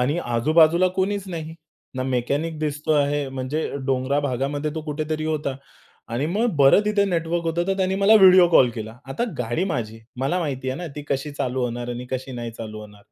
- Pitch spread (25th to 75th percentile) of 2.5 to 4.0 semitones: No, average, 4.6 semitones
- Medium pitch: Yes, medium, 145 Hz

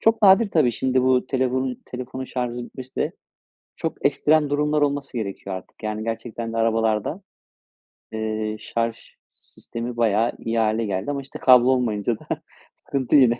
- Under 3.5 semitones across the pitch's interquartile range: Yes, average, 2.8 semitones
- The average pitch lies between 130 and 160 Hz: No, low, 120 Hz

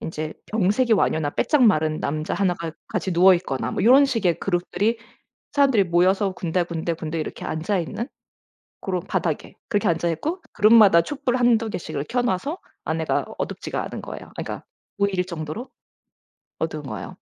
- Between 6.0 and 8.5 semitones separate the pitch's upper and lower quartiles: No, wide, 5.4 semitones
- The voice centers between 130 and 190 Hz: Yes, medium, 185 Hz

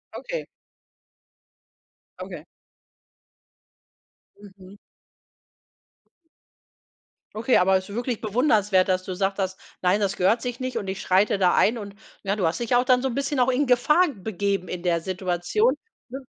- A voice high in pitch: Yes, high, 205 Hz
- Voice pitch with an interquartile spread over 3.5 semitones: Yes, average, 4.9 semitones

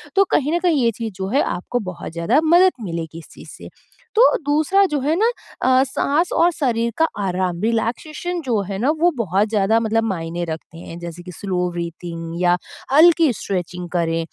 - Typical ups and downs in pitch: No, wide, 8.8 semitones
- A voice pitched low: No, high, 220 Hz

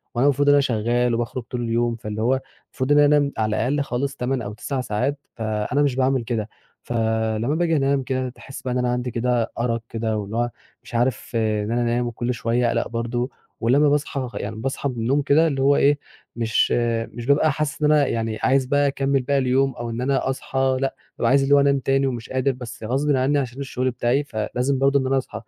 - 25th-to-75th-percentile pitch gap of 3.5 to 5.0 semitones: No, average, 3.0 semitones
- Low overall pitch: Yes, low, 125 Hz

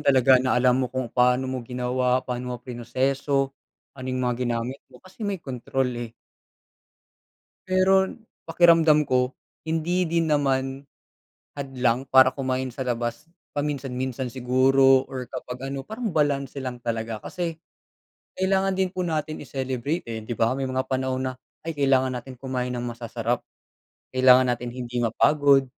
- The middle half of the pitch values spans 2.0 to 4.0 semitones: Yes, narrow, 2.5 semitones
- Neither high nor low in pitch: No, low, 130 Hz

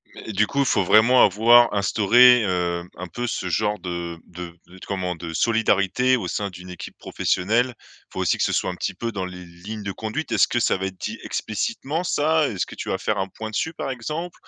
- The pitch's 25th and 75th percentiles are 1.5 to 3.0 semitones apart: No, average, 5.0 semitones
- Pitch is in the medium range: No, low, 105 Hz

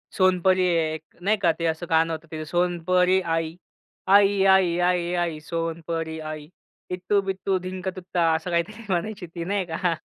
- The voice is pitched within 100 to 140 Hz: No, medium, 175 Hz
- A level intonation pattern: Yes, narrow, 2.2 semitones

